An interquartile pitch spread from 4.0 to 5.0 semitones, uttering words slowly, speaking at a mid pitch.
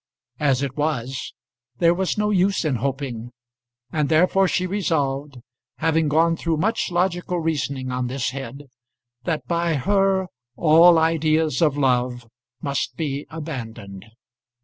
Yes: average, 4.3 semitones; slow, 130 wpm; medium, 155 Hz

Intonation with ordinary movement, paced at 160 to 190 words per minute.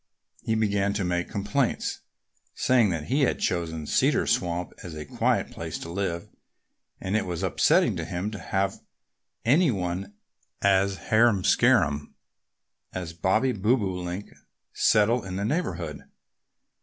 No: average, 3.6 semitones; slow, 135 wpm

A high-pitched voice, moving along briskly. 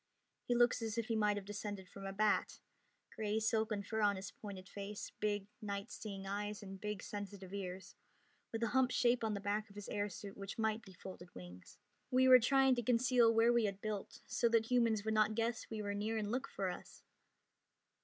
Yes: high, 210 Hz; fast, 215 wpm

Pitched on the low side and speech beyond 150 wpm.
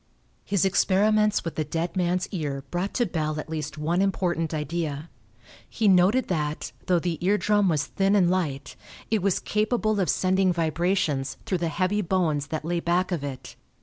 No: medium, 175 Hz; average, 180 wpm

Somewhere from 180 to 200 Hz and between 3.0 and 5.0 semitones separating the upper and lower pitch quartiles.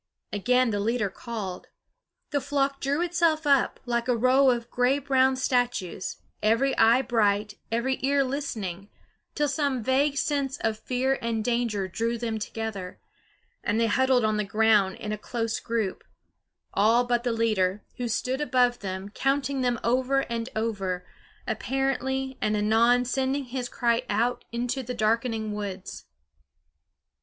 No: high, 240 Hz; average, 3.5 semitones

